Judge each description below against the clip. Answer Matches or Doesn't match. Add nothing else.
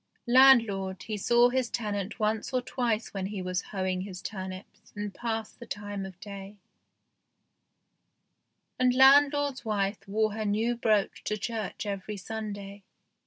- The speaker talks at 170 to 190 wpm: Doesn't match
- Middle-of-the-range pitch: Doesn't match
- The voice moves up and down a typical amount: Matches